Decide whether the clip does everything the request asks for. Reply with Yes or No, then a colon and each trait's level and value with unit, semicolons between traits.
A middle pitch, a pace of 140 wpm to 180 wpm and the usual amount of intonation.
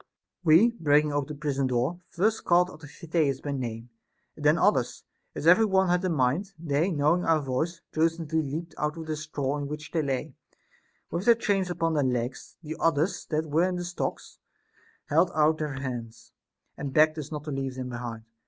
No: medium, 155 Hz; average, 195 wpm; average, 3.4 semitones